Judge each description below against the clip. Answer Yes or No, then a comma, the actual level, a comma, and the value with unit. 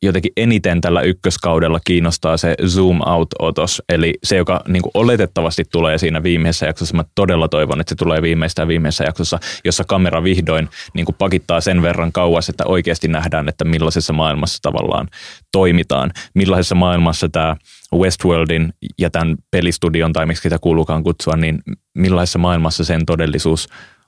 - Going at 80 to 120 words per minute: No, average, 150 wpm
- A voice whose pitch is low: Yes, very low, 85 Hz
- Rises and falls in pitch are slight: Yes, narrow, 1.9 semitones